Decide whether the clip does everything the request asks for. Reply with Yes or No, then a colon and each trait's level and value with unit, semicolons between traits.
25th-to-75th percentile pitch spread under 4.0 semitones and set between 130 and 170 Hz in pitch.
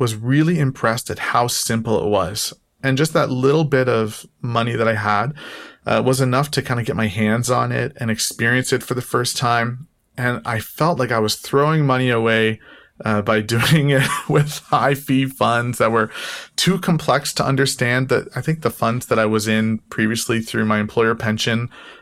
No: average, 3.3 semitones; low, 120 Hz